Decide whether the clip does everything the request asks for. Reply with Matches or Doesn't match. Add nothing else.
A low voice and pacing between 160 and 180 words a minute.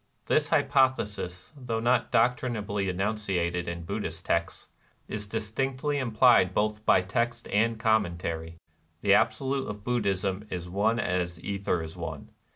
Doesn't match